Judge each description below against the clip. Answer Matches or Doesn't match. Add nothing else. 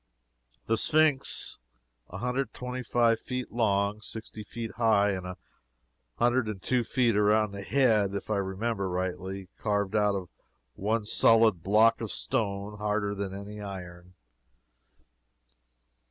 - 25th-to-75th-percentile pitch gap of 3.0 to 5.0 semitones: Doesn't match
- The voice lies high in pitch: Doesn't match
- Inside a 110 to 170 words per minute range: Matches